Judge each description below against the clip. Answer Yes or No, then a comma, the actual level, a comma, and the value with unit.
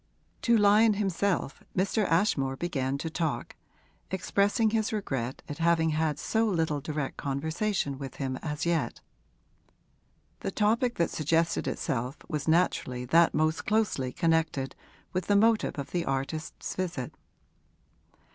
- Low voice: No, medium, 165 Hz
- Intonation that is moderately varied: No, wide, 6.1 semitones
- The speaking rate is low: Yes, slow, 130 wpm